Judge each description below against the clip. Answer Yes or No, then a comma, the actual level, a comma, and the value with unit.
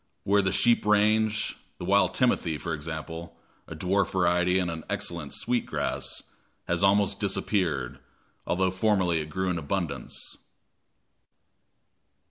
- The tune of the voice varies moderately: Yes, average, 3.3 semitones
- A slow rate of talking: Yes, slow, 125 wpm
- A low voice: Yes, very low, 95 Hz